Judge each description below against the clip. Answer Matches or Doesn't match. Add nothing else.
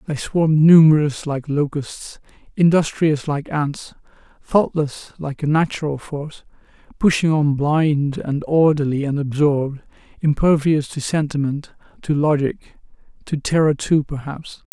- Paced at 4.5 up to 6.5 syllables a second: Doesn't match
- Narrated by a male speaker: Matches